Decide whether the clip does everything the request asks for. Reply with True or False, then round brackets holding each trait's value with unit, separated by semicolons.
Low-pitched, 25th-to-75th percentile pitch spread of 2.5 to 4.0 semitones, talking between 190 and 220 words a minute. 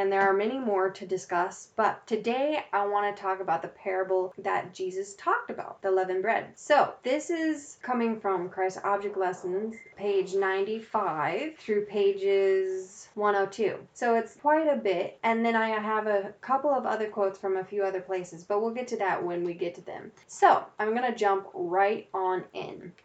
False (200 Hz; 2.9 semitones; 195 wpm)